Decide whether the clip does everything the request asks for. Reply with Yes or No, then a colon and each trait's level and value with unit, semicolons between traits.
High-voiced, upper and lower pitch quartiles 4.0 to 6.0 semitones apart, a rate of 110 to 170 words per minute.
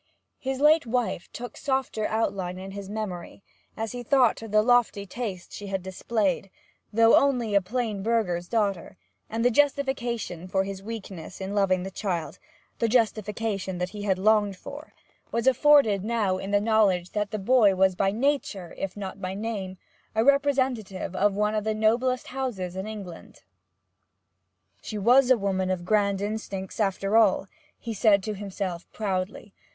No: high, 210 Hz; average, 3.3 semitones; average, 165 wpm